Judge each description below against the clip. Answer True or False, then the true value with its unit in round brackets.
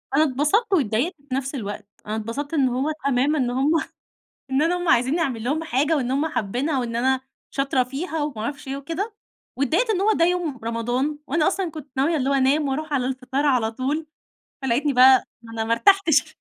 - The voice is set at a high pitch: True (275 Hz)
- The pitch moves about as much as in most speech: True (3.7 semitones)